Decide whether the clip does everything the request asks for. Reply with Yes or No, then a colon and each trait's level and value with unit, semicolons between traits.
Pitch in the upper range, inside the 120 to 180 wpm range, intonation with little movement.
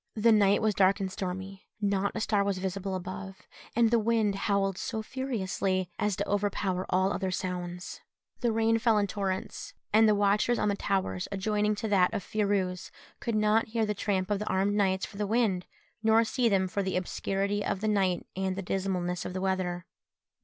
No: high, 200 Hz; average, 195 wpm; narrow, 2.1 semitones